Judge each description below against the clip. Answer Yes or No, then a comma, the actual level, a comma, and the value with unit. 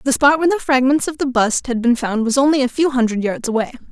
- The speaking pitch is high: Yes, very high, 260 Hz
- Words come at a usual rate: No, fast, 275 wpm